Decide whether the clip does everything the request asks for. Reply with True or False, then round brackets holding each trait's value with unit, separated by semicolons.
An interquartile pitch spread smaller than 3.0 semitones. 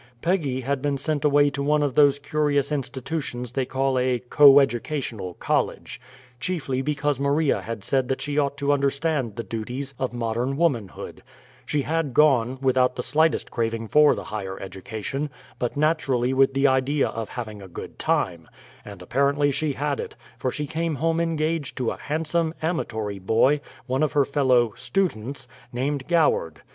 False (3.4 semitones)